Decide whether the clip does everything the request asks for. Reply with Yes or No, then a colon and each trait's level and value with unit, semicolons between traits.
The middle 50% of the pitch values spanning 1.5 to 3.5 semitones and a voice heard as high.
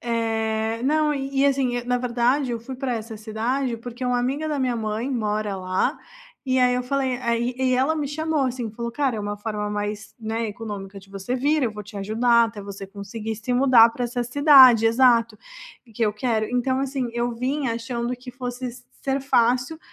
Yes: average, 2.9 semitones; high, 240 Hz